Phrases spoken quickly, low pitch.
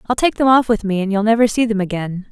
No: fast, 310 wpm; high, 215 Hz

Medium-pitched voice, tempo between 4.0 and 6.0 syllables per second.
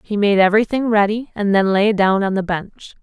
No: high, 205 Hz; 5.3 syllables/s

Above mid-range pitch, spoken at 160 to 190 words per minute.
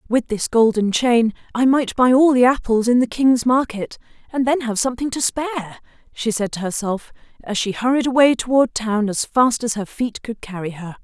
No: high, 235 Hz; fast, 205 wpm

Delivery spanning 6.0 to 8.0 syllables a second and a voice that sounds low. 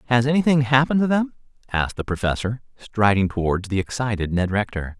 Yes: 6.1 syllables/s; low, 115 Hz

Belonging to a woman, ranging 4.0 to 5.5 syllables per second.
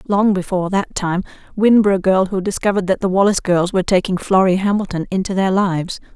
No: female; 6.4 syllables/s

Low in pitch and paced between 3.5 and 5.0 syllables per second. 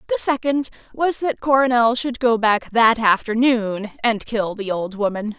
No: high, 235 Hz; 4.4 syllables/s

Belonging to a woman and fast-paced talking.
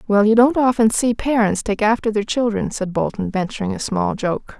Yes: female; fast, 210 wpm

